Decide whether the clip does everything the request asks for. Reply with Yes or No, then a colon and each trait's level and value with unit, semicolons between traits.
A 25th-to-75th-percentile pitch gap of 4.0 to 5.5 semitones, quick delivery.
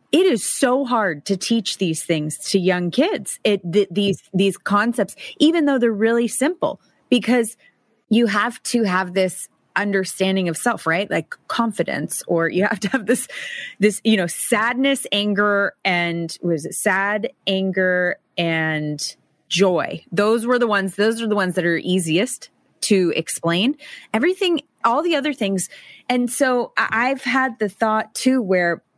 No: average, 5.1 semitones; average, 160 wpm